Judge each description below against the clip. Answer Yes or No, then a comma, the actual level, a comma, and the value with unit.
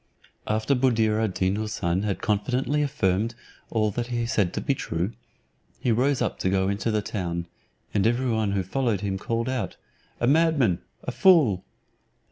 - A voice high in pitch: No, low, 110 Hz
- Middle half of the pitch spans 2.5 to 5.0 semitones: Yes, average, 4.1 semitones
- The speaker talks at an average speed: Yes, average, 170 wpm